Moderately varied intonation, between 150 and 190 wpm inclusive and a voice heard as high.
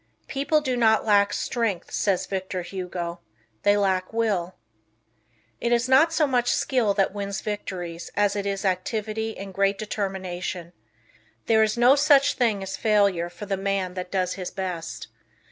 Yes: average, 3.3 semitones; average, 160 wpm; high, 200 Hz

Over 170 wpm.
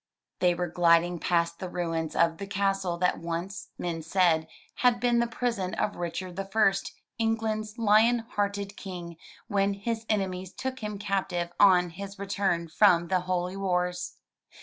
No: average, 155 wpm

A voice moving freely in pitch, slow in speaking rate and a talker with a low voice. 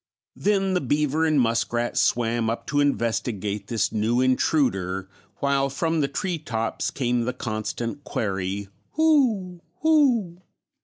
Yes: wide, 6.4 semitones; slow, 125 wpm; low, 130 Hz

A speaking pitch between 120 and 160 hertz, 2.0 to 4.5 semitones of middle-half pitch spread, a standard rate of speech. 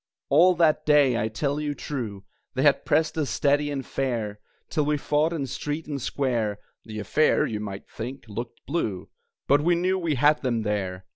No: medium, 140 Hz; average, 5.2 semitones; average, 190 wpm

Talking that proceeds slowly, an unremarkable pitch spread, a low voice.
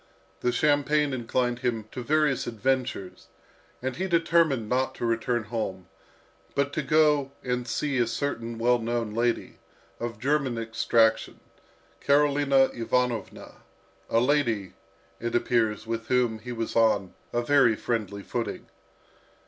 Yes: slow, 130 wpm; average, 3.3 semitones; low, 120 Hz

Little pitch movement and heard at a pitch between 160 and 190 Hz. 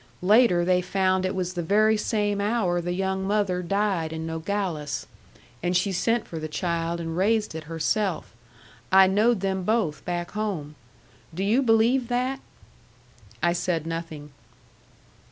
No: average, 3.8 semitones; medium, 185 Hz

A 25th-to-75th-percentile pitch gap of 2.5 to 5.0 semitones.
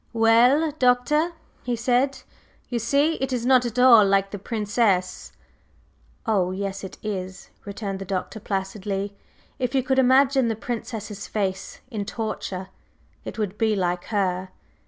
Yes: average, 4.2 semitones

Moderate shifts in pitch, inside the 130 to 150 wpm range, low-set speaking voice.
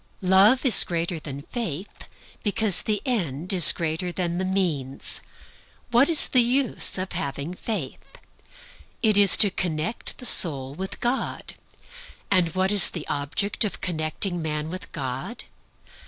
No: average, 5.0 semitones; average, 140 wpm; medium, 185 Hz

